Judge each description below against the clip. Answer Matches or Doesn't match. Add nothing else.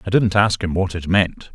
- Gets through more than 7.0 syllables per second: Doesn't match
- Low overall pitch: Matches